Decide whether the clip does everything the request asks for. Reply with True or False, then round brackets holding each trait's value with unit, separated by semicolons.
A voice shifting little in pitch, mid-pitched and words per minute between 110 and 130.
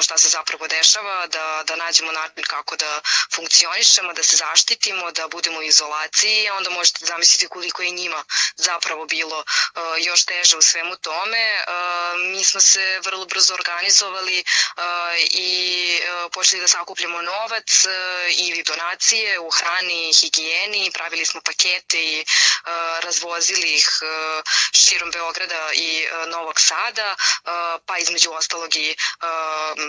True (1.9 semitones; 170 Hz; 125 wpm)